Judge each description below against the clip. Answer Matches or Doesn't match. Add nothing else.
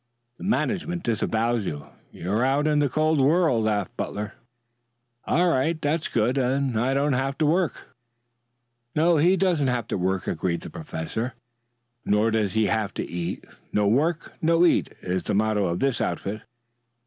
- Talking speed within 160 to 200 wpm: Matches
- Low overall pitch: Matches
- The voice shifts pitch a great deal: Matches